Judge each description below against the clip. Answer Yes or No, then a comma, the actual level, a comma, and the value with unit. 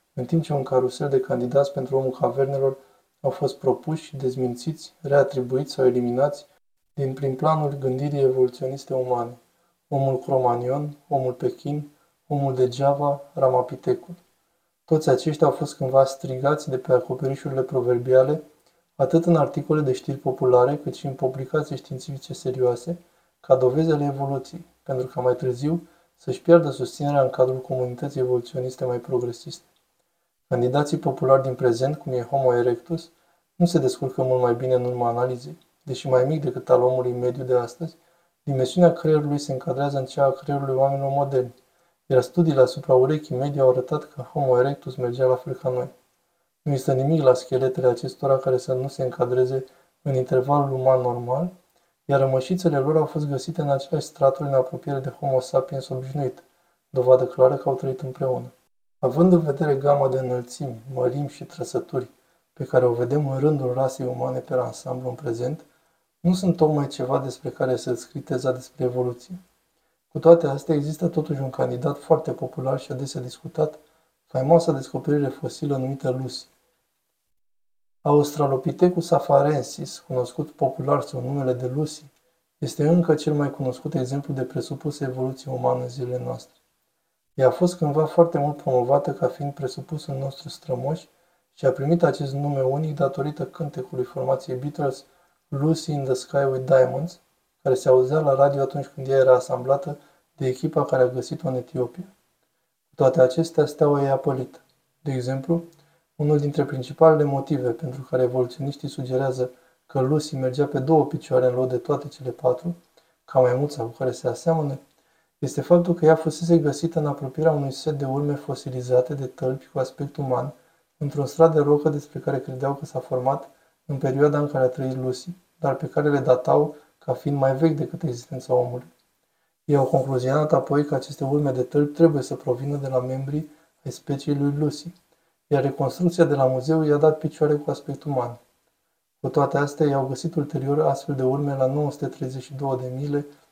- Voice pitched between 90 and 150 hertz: Yes, medium, 140 Hz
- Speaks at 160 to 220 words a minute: Yes, average, 165 wpm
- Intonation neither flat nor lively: Yes, average, 3.8 semitones